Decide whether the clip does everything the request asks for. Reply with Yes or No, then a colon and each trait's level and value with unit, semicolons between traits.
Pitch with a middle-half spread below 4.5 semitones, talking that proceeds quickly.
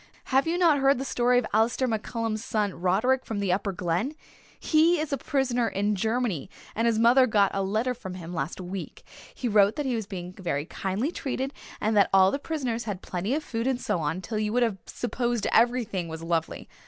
No: average, 4.8 semitones; fast, 215 wpm